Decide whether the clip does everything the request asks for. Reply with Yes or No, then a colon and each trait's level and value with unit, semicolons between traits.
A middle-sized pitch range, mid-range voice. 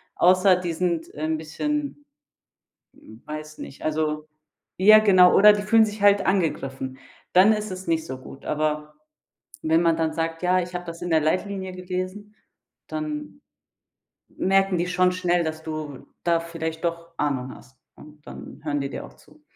Yes: average, 3.4 semitones; medium, 170 Hz